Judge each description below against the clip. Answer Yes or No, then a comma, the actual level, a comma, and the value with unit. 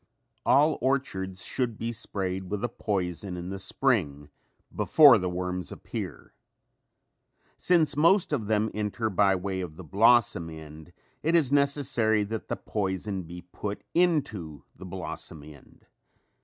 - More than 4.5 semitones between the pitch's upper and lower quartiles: Yes, average, 5.3 semitones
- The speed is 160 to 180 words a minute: No, average, 140 wpm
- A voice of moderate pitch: No, low, 100 Hz